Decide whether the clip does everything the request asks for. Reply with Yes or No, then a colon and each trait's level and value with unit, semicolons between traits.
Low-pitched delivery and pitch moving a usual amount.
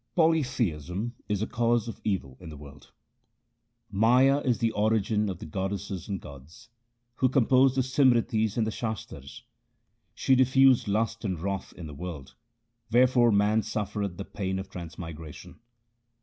Yes: low, 105 Hz; average, 4.9 semitones